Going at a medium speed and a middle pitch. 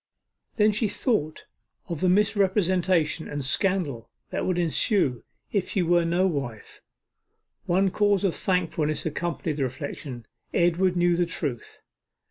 No: slow, 130 wpm; medium, 175 Hz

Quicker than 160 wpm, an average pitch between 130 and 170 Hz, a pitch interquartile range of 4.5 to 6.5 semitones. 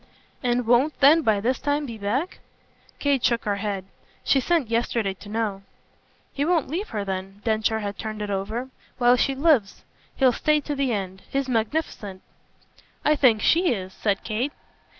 No: average, 170 wpm; high, 235 Hz; average, 5.3 semitones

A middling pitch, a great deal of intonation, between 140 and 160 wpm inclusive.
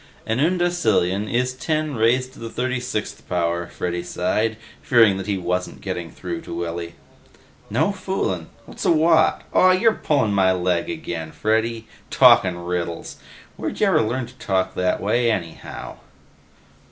No: low, 110 Hz; wide, 6.3 semitones; average, 150 wpm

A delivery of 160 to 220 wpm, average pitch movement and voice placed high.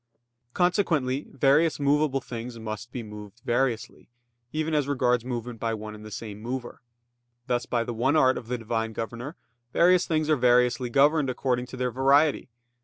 No: average, 170 wpm; average, 3.4 semitones; low, 125 Hz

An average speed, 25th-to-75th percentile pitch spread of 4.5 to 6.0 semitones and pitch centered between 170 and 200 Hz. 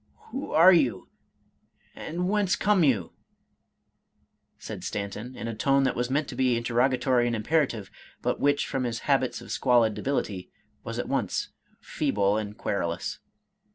No: average, 155 wpm; average, 4.9 semitones; low, 125 Hz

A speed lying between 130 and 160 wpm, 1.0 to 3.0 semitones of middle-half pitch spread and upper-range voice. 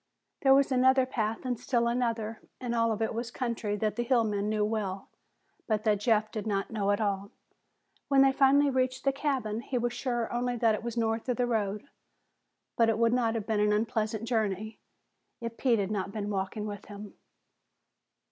No: average, 200 wpm; narrow, 2.6 semitones; high, 225 Hz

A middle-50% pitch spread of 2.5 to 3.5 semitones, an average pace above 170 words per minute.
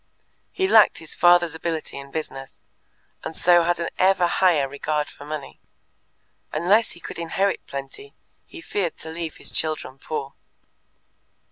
No: average, 2.9 semitones; average, 145 wpm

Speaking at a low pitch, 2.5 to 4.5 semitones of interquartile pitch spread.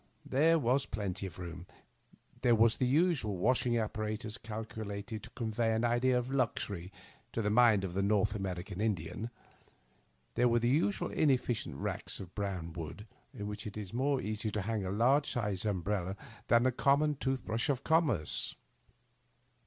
Yes: low, 110 Hz; average, 3.8 semitones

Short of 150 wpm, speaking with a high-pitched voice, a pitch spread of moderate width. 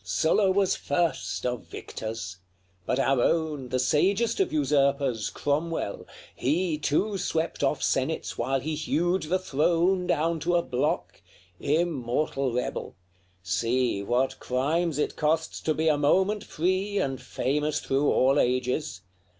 No: average, 140 wpm; medium, 150 Hz; average, 4.7 semitones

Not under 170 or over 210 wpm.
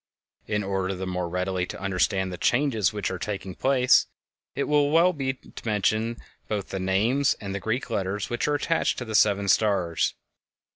Yes: average, 185 wpm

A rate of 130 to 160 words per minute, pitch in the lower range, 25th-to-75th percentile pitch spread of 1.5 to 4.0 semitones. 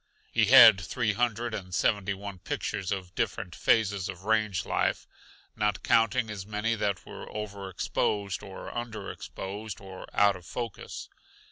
Yes: average, 150 wpm; low, 105 Hz; narrow, 2.5 semitones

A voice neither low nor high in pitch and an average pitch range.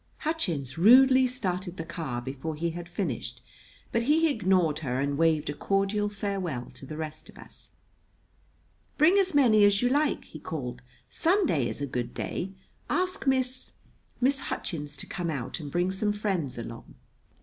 No: medium, 180 Hz; wide, 8.9 semitones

